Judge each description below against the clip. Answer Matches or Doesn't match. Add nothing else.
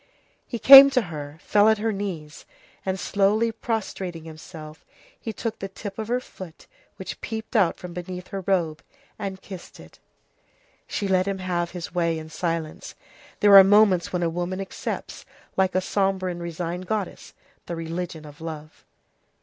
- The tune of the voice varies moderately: Matches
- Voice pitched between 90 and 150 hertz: Doesn't match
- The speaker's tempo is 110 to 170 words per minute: Matches